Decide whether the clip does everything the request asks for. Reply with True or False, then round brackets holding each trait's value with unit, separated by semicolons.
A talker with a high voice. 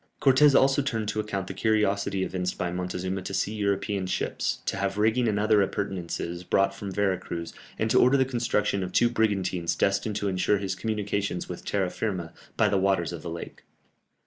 False (100 Hz)